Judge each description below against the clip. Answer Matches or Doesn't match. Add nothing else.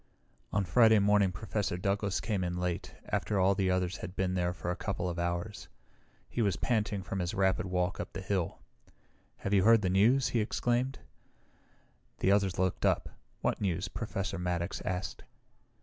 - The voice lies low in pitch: Matches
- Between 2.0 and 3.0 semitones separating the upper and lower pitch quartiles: Matches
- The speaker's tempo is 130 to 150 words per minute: Doesn't match